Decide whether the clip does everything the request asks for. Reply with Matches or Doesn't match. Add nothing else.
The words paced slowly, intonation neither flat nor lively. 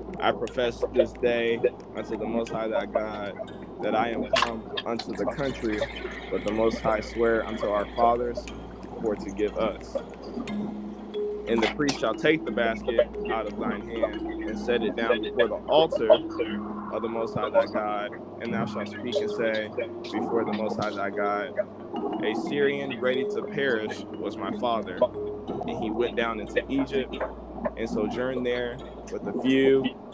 Doesn't match